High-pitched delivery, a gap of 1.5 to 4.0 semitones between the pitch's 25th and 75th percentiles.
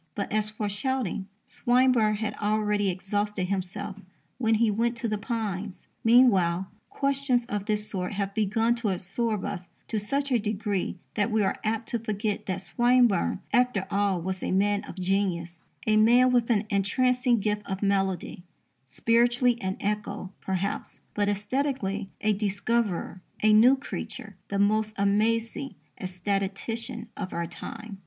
Yes: high, 210 Hz; average, 2.9 semitones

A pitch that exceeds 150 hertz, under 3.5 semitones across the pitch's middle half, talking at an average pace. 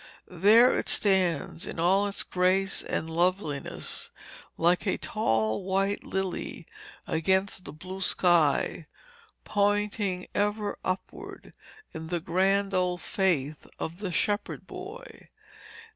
No: high, 190 Hz; average, 2.8 semitones; slow, 115 wpm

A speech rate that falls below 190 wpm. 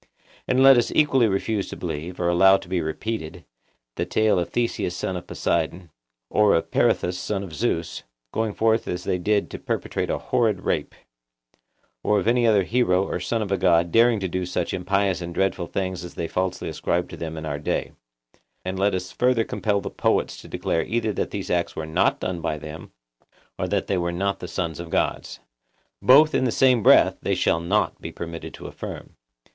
No: fast, 205 wpm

